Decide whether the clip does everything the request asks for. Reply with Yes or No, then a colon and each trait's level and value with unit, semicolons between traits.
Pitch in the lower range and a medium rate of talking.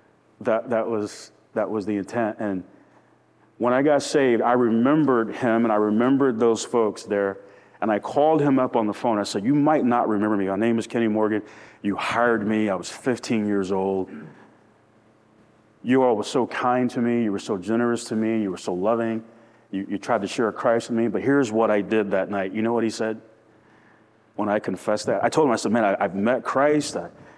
No: low, 110 Hz; fast, 225 wpm